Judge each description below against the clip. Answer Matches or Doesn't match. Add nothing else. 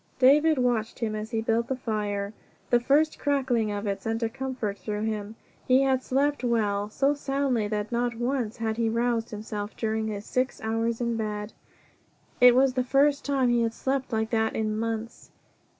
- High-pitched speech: Matches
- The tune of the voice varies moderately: Matches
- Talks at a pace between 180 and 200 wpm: Matches